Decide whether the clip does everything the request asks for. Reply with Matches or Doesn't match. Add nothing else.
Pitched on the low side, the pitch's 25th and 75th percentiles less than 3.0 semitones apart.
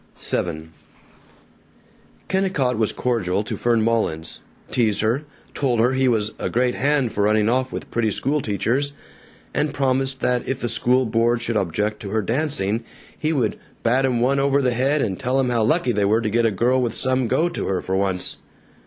Doesn't match